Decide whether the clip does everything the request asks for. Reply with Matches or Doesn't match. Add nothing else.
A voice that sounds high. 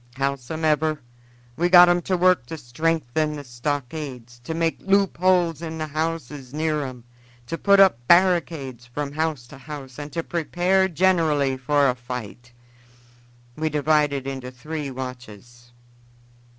Doesn't match